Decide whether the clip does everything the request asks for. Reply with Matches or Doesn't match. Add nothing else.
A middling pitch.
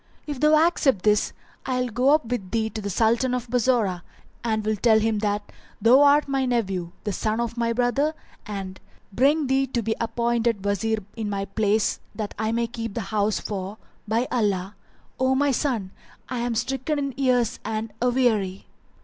Doesn't match